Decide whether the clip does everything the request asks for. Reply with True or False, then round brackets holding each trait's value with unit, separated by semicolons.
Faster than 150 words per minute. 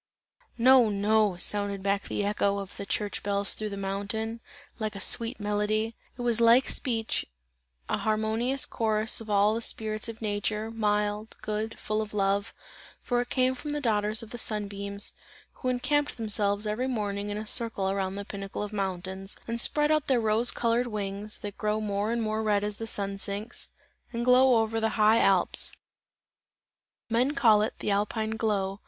True (185 wpm)